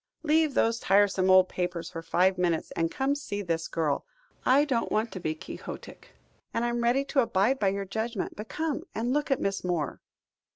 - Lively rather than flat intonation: Yes, wide, 5.8 semitones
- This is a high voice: Yes, high, 205 Hz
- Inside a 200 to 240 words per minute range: Yes, fast, 205 wpm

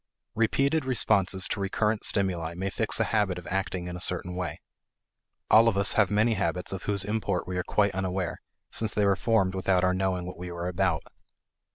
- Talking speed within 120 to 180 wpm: No, average, 200 wpm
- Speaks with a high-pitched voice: No, very low, 95 Hz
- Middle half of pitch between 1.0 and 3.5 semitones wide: Yes, average, 2.7 semitones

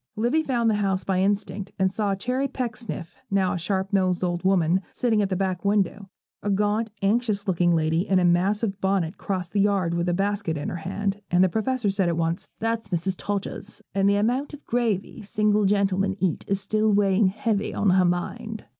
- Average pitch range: No, narrow, 2.3 semitones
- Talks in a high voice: Yes, high, 195 Hz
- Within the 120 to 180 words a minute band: No, average, 200 wpm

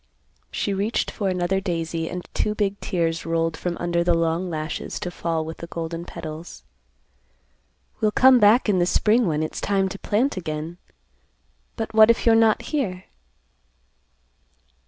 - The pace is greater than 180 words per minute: No, average, 155 wpm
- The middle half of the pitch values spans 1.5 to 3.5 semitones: No, average, 4.0 semitones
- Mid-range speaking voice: Yes, medium, 180 Hz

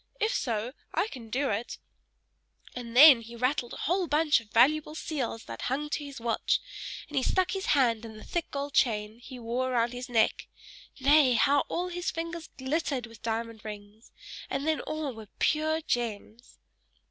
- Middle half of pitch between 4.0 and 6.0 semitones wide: Yes, average, 4.8 semitones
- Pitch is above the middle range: Yes, very high, 255 Hz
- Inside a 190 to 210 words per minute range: No, average, 180 wpm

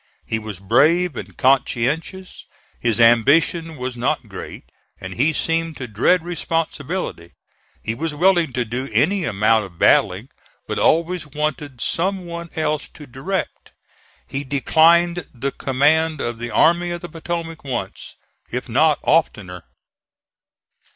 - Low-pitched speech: No, medium, 150 Hz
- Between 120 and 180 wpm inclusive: Yes, slow, 135 wpm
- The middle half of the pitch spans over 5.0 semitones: Yes, wide, 5.5 semitones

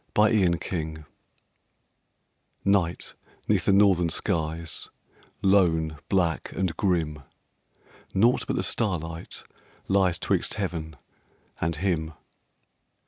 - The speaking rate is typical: No, slow, 90 wpm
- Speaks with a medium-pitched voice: No, very low, 85 Hz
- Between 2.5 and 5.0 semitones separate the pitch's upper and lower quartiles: Yes, average, 3.3 semitones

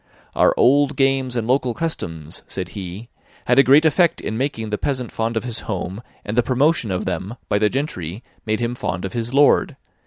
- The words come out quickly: Yes, fast, 210 wpm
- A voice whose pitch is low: Yes, low, 120 Hz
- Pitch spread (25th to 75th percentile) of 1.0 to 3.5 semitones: No, average, 4.7 semitones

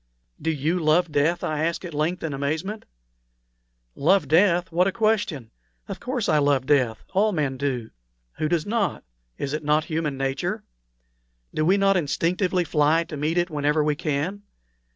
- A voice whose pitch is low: No, medium, 155 Hz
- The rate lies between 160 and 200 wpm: Yes, average, 170 wpm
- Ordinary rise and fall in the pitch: Yes, average, 3.7 semitones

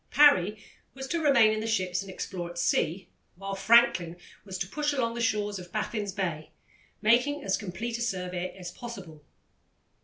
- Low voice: No, high, 205 Hz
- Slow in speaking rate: No, average, 175 wpm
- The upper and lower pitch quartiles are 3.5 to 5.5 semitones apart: Yes, average, 4.5 semitones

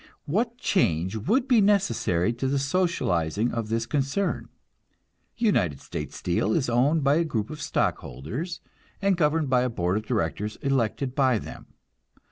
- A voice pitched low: Yes, low, 130 Hz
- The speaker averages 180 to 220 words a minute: No, average, 150 wpm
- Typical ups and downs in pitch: No, wide, 7.4 semitones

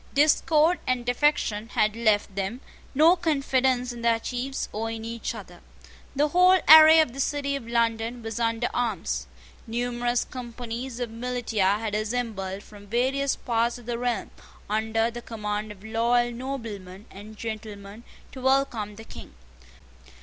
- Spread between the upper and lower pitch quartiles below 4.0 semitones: Yes, average, 2.7 semitones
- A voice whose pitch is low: No, high, 235 Hz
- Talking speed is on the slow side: No, average, 150 wpm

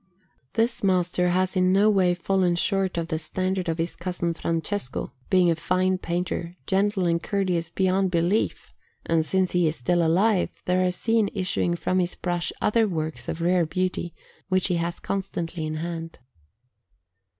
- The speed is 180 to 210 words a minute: No, average, 165 wpm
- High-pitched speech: No, medium, 180 Hz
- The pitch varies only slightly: Yes, narrow, 1.9 semitones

